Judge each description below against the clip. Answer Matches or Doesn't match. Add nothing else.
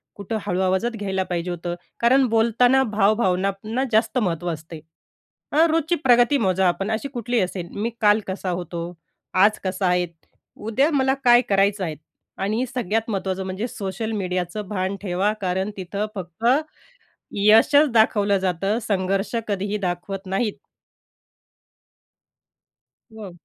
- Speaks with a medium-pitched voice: Doesn't match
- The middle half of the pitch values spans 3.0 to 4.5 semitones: Matches